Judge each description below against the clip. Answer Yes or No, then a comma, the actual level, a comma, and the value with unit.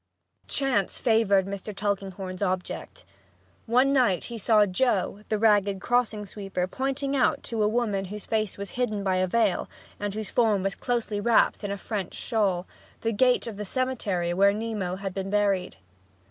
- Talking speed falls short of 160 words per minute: No, average, 170 wpm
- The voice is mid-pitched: No, high, 205 Hz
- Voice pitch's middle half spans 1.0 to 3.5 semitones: Yes, average, 2.9 semitones